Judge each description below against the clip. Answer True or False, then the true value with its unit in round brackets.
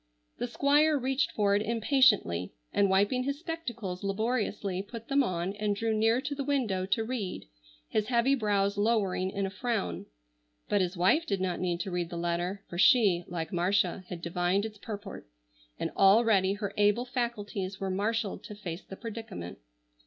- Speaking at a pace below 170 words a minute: False (175 wpm)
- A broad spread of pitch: False (4.0 semitones)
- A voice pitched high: True (205 Hz)